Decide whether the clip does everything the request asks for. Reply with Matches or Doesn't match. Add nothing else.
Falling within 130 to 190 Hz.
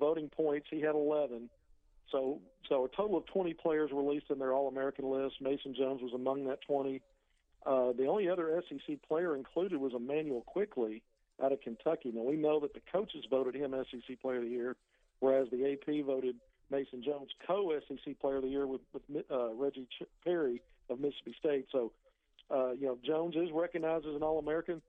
Matches